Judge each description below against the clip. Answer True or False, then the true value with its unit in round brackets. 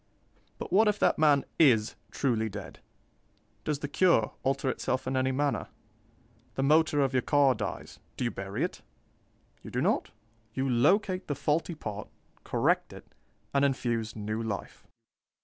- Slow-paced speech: False (155 wpm)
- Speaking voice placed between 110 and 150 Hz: True (135 Hz)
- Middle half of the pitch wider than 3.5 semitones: True (4.5 semitones)